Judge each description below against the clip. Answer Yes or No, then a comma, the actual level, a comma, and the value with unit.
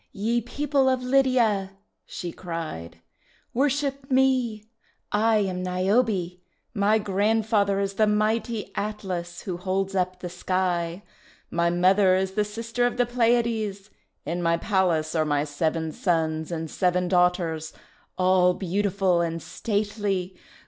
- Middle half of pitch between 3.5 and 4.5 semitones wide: Yes, average, 3.9 semitones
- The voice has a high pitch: Yes, high, 195 Hz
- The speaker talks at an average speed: No, slow, 130 wpm